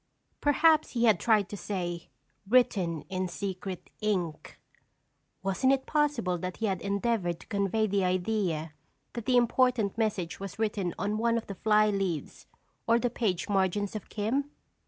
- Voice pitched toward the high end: Yes, high, 205 Hz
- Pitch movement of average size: Yes, average, 3.9 semitones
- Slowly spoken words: No, average, 155 wpm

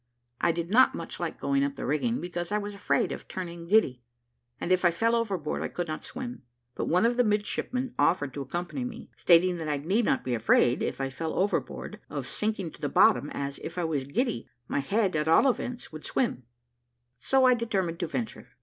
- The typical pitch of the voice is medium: Yes, medium, 180 Hz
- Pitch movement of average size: No, wide, 6.7 semitones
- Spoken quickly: Yes, fast, 215 wpm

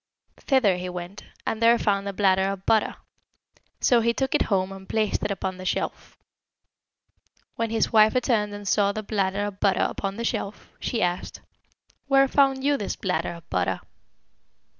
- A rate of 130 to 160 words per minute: No, average, 175 wpm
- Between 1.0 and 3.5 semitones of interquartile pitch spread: Yes, average, 3.2 semitones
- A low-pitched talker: No, high, 205 Hz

